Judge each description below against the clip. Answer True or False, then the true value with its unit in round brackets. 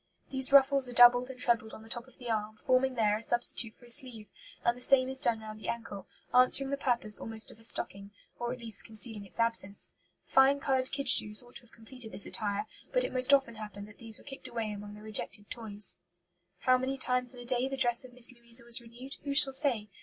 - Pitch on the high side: True (240 Hz)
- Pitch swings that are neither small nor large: True (3.0 semitones)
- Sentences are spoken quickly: True (240 wpm)